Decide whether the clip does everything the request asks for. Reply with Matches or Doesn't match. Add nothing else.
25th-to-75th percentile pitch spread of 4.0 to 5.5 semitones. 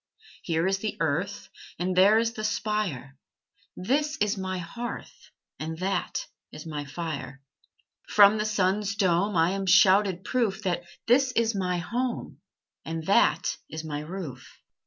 Matches